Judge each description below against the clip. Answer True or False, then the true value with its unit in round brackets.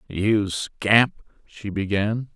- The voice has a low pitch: True (105 Hz)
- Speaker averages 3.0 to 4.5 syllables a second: True (3.6 syllables/s)